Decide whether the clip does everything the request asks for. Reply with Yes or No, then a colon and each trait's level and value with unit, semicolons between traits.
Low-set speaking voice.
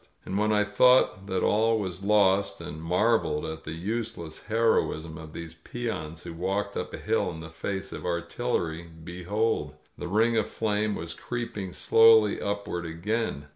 Yes: very low, 95 Hz